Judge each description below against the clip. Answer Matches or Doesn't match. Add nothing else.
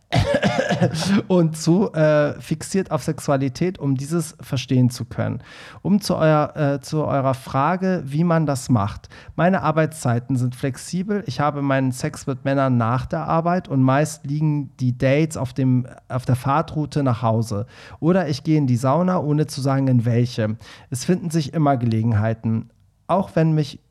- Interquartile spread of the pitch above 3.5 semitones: Matches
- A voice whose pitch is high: Doesn't match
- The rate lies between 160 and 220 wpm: Matches